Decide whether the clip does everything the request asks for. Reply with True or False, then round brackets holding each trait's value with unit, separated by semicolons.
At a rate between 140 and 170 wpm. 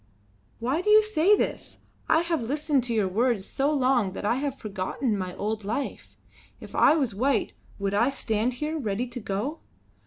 False (185 wpm)